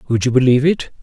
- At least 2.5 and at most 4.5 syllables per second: No, 7.6 syllables/s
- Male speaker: Yes, male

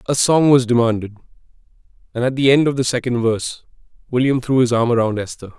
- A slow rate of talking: No, average, 195 wpm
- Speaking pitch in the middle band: No, low, 125 Hz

